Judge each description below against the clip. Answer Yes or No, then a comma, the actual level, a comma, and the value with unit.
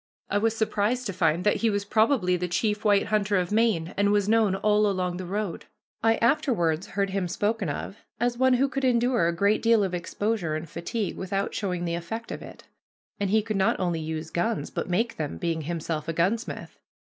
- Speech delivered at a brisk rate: Yes, fast, 210 wpm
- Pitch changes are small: No, average, 4.3 semitones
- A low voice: No, high, 200 Hz